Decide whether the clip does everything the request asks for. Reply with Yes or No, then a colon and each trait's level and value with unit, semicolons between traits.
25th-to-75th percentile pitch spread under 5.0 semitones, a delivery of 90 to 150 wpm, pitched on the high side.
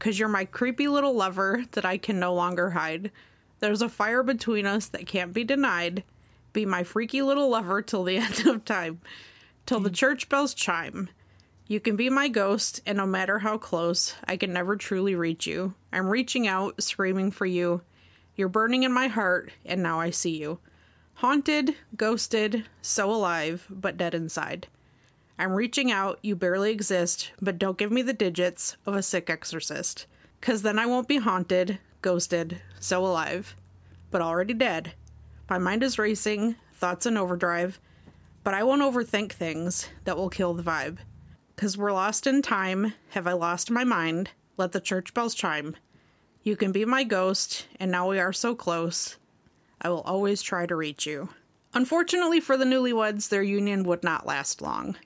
No: average, 4.1 semitones; average, 180 wpm; high, 195 Hz